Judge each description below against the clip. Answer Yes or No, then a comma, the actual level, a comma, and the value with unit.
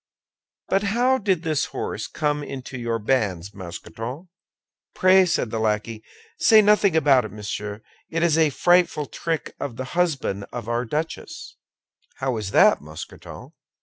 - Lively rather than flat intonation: Yes, wide, 7.6 semitones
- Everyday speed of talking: Yes, average, 150 wpm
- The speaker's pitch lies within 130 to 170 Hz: Yes, low, 135 Hz